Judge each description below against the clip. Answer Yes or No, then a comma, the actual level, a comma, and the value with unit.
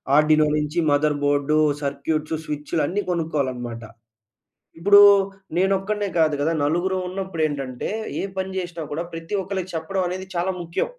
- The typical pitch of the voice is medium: Yes, medium, 165 Hz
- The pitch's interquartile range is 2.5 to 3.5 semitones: No, average, 4.1 semitones